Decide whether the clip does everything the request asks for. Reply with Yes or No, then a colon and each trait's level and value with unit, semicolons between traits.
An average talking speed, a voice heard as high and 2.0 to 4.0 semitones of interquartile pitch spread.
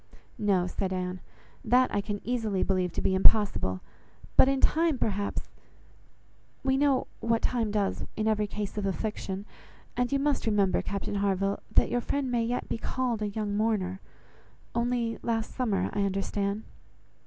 Yes: average, 155 wpm; high, 210 Hz; average, 3.4 semitones